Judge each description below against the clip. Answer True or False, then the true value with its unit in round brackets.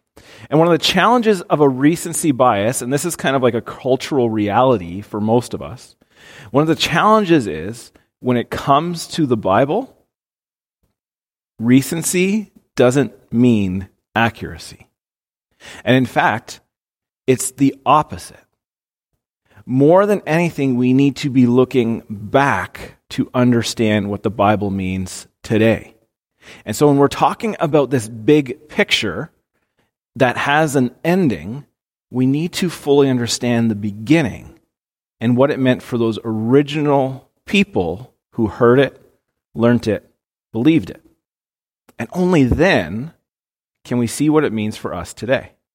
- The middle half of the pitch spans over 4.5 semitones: True (4.9 semitones)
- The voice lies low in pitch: True (130 Hz)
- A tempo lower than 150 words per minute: True (140 wpm)